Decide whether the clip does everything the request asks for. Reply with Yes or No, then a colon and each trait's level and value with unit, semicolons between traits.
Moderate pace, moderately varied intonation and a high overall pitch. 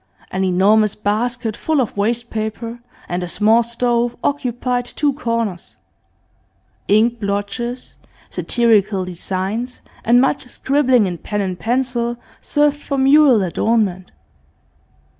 No: slow, 115 wpm; average, 3.4 semitones; high, 230 Hz